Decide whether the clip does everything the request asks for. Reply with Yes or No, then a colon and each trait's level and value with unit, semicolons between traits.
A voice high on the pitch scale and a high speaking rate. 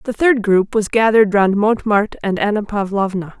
No: high, 210 Hz; average, 175 wpm